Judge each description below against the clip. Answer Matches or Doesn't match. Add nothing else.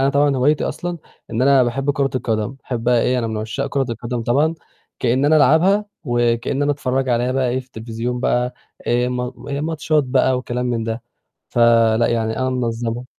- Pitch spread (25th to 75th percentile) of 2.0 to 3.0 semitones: Matches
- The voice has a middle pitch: Doesn't match